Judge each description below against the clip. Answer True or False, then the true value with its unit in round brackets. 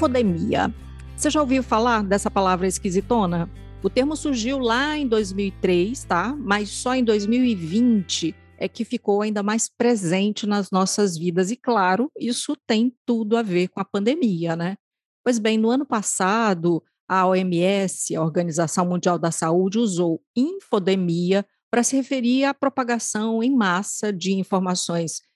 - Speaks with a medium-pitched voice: False (210 Hz)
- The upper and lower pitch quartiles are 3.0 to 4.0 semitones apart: False (4.6 semitones)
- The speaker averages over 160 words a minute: False (145 wpm)